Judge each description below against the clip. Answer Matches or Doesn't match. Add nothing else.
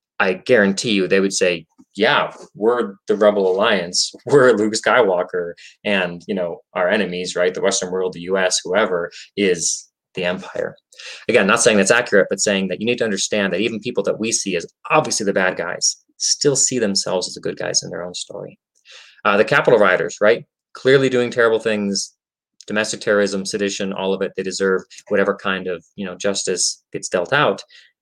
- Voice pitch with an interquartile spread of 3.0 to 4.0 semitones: Matches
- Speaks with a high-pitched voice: Doesn't match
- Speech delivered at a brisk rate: Doesn't match